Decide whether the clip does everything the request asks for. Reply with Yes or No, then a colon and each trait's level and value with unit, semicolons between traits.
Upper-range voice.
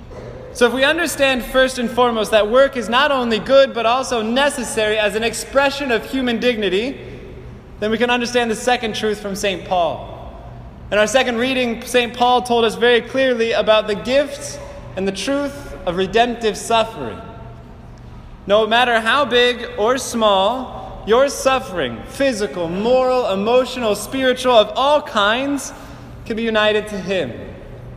Yes: high, 240 Hz